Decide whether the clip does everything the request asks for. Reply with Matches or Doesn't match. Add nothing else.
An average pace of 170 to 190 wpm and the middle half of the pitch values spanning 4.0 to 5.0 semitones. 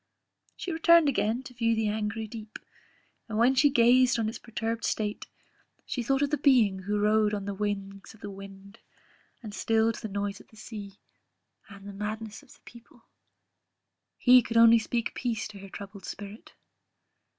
Doesn't match